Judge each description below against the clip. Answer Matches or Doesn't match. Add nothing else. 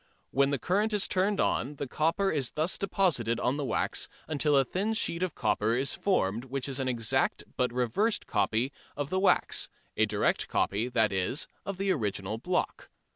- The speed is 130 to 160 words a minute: Doesn't match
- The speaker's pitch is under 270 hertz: Matches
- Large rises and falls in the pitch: Matches